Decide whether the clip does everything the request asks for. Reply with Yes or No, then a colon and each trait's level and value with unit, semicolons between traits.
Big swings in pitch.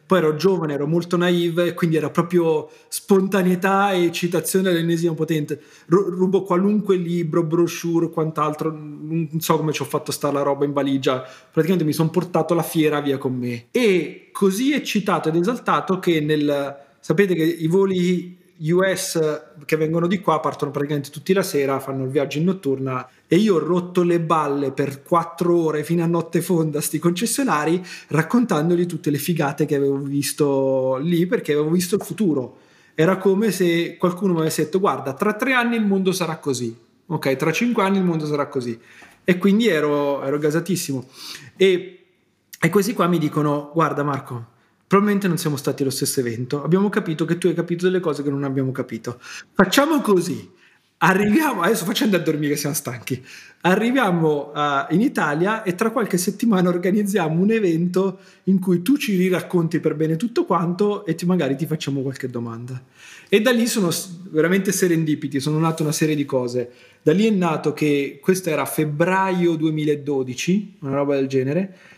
No: average, 4.3 semitones